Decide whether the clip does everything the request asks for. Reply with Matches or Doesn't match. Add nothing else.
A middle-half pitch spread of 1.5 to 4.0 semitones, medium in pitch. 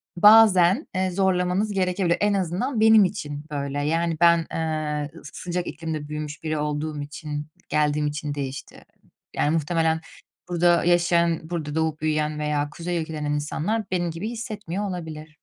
Matches